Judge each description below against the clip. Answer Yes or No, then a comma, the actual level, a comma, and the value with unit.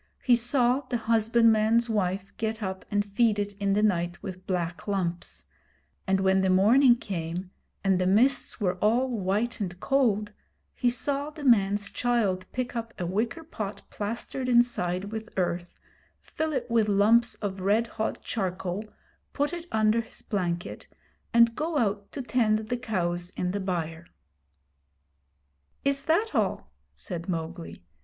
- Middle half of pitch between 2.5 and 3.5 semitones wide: No, average, 4.2 semitones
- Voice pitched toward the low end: No, high, 210 Hz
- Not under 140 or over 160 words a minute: Yes, average, 150 wpm